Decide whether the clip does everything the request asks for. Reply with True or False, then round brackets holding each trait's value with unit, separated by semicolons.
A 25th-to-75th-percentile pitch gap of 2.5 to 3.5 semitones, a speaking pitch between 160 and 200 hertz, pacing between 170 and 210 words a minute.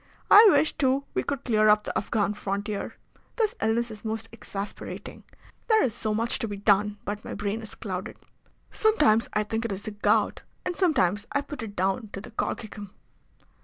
False (3.0 semitones; 215 Hz; 190 wpm)